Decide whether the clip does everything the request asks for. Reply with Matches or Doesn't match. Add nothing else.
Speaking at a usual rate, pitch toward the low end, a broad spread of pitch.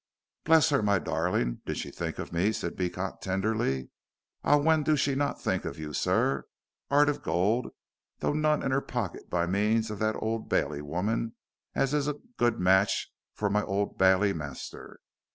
Matches